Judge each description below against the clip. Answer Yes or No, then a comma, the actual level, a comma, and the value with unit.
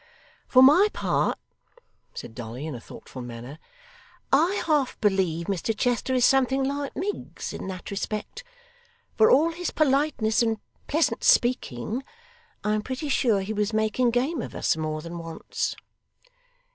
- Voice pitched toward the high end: Yes, high, 225 Hz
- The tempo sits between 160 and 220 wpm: No, average, 145 wpm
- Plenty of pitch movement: Yes, wide, 7.4 semitones